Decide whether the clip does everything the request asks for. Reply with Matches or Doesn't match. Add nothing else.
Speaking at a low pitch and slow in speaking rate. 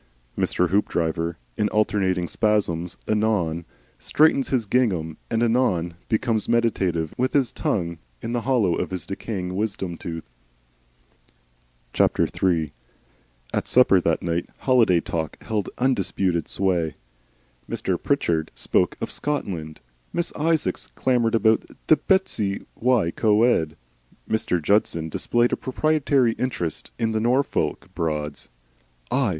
Matches